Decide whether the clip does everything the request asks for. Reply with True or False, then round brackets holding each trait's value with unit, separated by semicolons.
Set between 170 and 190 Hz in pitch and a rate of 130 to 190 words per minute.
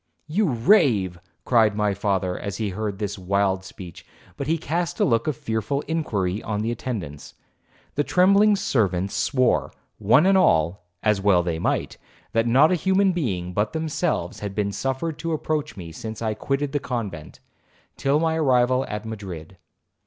False (110 Hz; 165 wpm)